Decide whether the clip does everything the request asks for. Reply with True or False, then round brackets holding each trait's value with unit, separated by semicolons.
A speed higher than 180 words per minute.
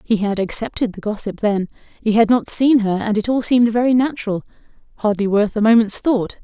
True (195 wpm)